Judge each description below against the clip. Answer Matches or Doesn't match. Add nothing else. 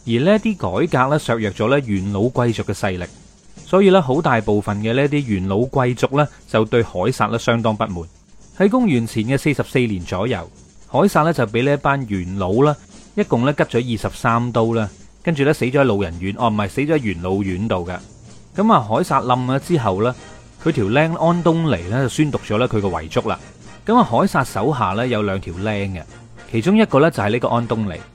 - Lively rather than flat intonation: Matches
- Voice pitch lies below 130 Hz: Matches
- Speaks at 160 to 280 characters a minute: Doesn't match